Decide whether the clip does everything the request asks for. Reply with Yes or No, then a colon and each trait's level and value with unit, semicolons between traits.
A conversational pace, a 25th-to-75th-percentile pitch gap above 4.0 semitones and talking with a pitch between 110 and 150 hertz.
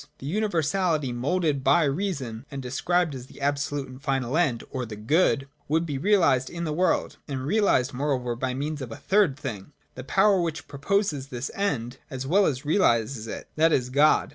Yes: average, 190 wpm; average, 4.5 semitones; medium, 140 Hz